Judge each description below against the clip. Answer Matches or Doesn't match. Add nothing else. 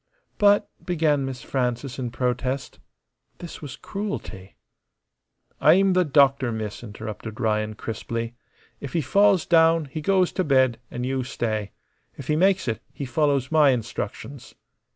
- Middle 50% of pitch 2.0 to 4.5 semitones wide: Doesn't match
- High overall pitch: Doesn't match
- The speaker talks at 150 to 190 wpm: Doesn't match